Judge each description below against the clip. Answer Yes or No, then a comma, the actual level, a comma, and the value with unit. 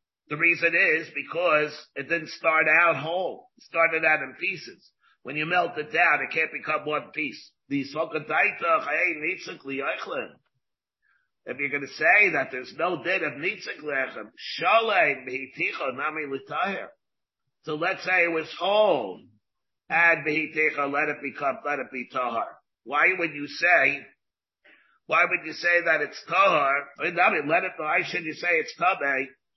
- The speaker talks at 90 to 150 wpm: Yes, average, 140 wpm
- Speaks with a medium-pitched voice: Yes, medium, 155 Hz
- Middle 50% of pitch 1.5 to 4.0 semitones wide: Yes, average, 2.8 semitones